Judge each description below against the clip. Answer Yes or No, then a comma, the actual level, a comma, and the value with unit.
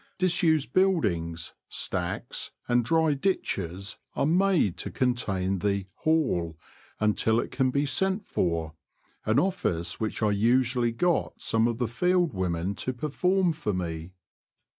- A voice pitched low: Yes, low, 120 Hz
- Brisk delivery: No, average, 145 wpm